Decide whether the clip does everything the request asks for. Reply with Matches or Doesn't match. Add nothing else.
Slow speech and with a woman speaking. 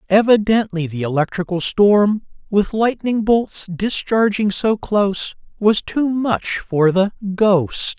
Doesn't match